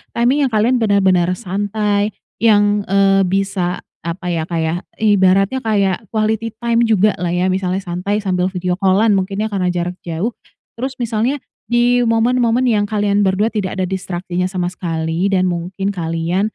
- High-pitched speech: Yes, high, 195 Hz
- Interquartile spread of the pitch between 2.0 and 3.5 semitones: Yes, average, 3.0 semitones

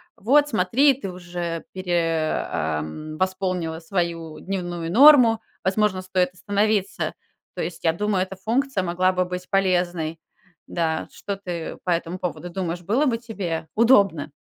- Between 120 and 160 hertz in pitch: No, medium, 185 Hz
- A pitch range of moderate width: Yes, average, 3.2 semitones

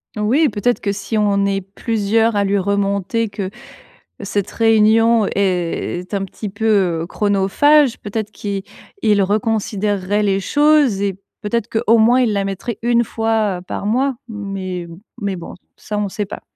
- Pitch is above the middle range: Yes, high, 205 Hz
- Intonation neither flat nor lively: No, narrow, 2.3 semitones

